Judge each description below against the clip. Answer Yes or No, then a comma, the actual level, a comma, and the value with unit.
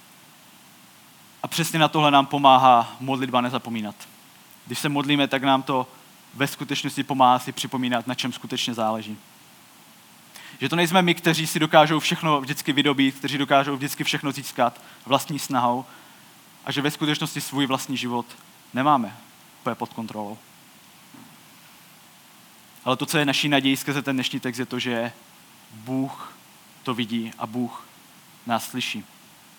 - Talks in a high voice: No, low, 135 Hz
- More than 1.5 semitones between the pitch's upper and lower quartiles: Yes, narrow, 2.6 semitones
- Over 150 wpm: No, average, 145 wpm